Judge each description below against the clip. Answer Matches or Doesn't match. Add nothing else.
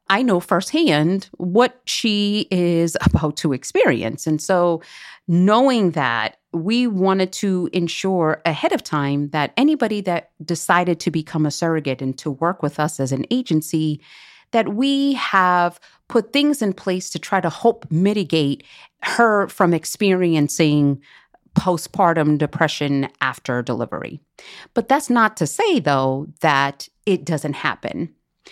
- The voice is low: Doesn't match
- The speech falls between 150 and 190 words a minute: Doesn't match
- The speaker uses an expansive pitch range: Doesn't match